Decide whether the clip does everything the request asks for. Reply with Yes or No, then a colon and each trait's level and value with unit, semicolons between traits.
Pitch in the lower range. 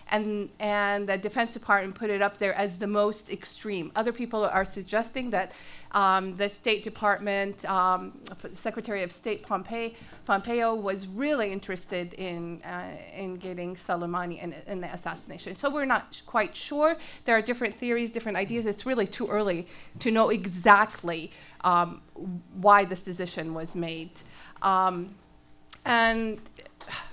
No: high, 200 Hz